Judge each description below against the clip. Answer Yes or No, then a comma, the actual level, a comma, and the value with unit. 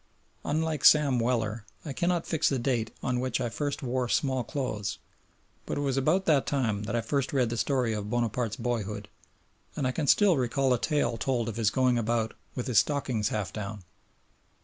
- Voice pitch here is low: Yes, low, 125 Hz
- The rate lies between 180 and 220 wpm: Yes, average, 195 wpm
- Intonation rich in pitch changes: No, average, 3.6 semitones